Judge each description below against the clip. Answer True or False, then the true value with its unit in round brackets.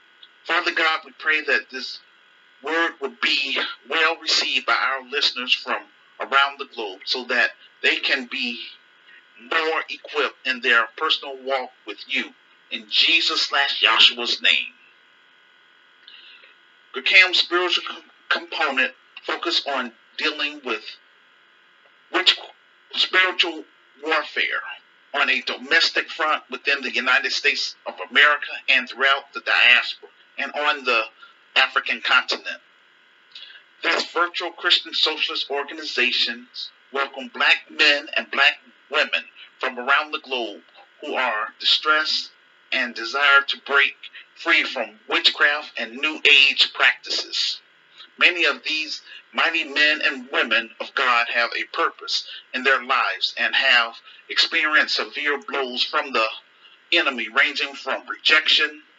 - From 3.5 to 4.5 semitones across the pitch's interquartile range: False (5.0 semitones)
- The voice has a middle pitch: True (155 Hz)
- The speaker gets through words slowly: True (120 wpm)